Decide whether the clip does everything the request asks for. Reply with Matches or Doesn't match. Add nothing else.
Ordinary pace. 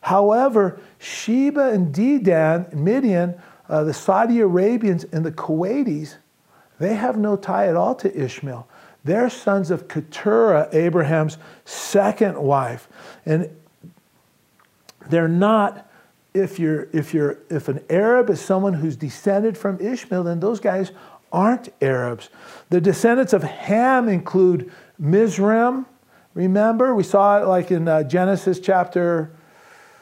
Doesn't match